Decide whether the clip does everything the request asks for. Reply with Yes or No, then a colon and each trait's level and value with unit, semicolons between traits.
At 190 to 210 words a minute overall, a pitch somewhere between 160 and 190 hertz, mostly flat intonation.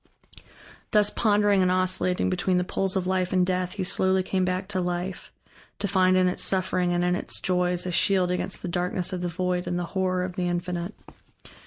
Yes: fast, 205 wpm; medium, 185 Hz; narrow, 0.9 semitones